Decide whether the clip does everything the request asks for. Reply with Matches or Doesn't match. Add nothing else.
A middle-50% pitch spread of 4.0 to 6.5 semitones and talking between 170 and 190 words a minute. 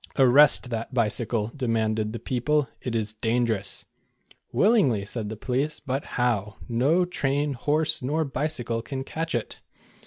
Doesn't match